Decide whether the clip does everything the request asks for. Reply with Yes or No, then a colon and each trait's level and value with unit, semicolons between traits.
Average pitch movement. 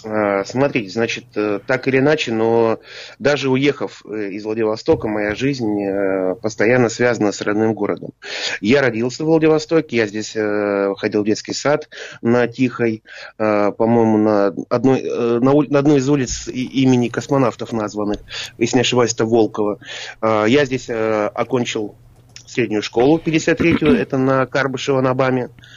Yes: average, 3.6 semitones